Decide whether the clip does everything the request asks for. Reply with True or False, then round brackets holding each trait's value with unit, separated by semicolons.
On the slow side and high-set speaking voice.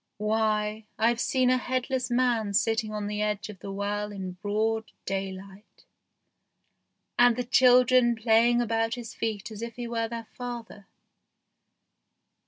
False (145 wpm; 225 Hz)